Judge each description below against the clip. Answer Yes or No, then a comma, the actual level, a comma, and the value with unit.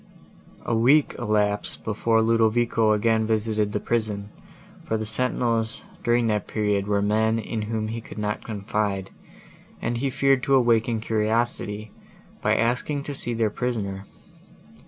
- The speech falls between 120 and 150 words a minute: Yes, average, 140 wpm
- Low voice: Yes, low, 110 Hz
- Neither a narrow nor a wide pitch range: No, narrow, 1.9 semitones